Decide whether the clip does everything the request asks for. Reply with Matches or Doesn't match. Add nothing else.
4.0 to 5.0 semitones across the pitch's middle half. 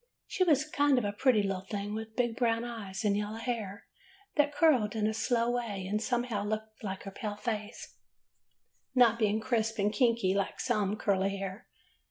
Doesn't match